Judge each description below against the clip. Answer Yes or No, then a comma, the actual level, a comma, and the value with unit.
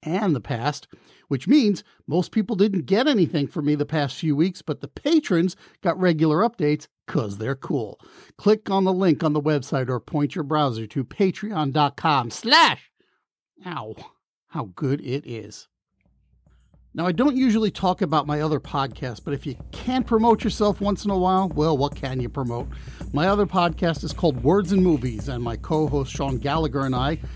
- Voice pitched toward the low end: No, medium, 155 Hz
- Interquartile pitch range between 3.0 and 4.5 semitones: No, average, 5.2 semitones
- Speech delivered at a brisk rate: No, average, 180 wpm